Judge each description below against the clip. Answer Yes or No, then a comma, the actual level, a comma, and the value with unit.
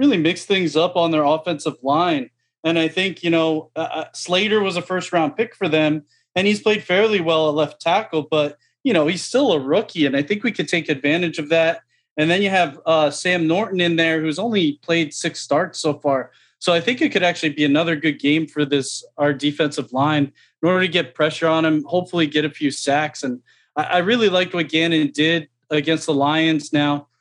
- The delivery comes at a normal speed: No, fast, 220 wpm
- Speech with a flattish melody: No, average, 3.0 semitones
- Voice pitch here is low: No, medium, 160 Hz